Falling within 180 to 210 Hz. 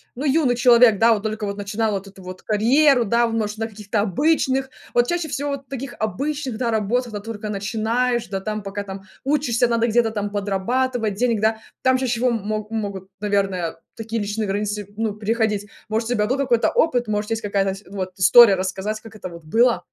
No: high, 220 Hz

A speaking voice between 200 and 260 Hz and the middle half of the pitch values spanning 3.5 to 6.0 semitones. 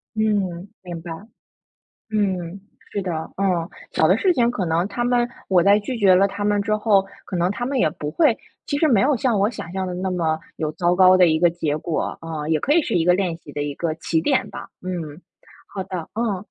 No: medium, 185 Hz; average, 3.8 semitones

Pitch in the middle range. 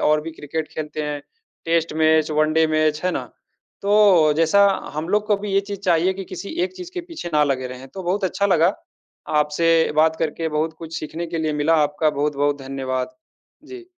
Yes: medium, 160 Hz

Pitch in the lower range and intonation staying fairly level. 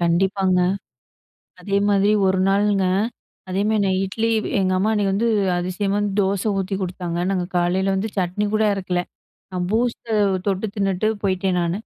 No: high, 195 Hz; narrow, 1.8 semitones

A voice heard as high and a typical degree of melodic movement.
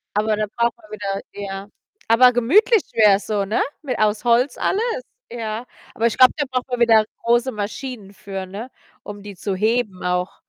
Yes: high, 220 Hz; average, 3.3 semitones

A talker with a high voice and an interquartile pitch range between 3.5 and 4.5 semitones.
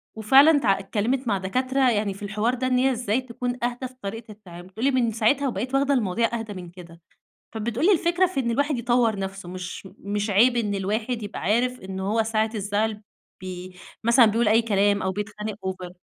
Yes: high, 220 Hz; average, 3.9 semitones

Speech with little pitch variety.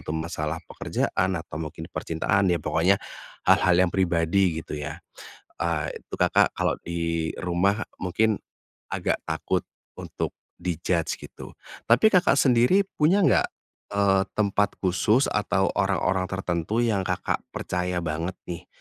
No: average, 3.3 semitones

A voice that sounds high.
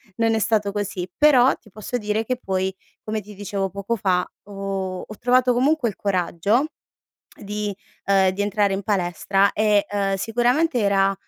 Yes: high, 205 Hz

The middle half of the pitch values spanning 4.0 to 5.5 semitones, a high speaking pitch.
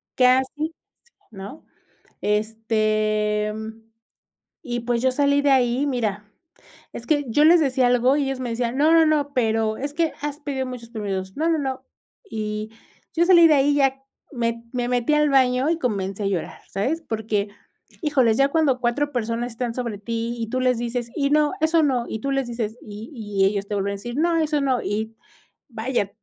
Yes: average, 4.4 semitones; high, 245 Hz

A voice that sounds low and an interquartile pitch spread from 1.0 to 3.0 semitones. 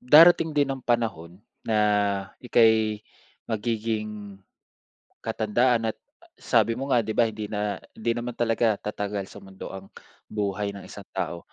Yes: low, 110 Hz; narrow, 2.5 semitones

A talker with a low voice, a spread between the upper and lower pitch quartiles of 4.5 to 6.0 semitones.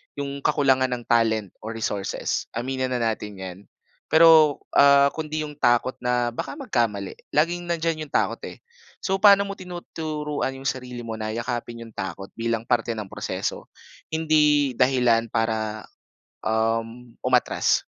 Yes: low, 125 Hz; average, 4.8 semitones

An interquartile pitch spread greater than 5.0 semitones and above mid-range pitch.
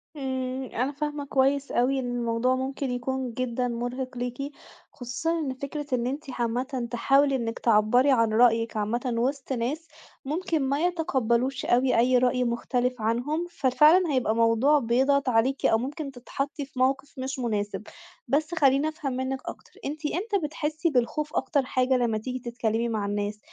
No: average, 2.9 semitones; very high, 255 Hz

